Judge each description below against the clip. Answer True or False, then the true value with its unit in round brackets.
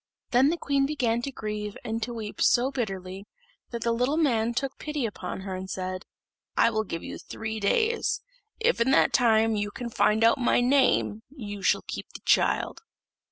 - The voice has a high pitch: True (230 Hz)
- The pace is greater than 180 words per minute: True (190 wpm)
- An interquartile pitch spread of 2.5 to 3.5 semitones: False (4.1 semitones)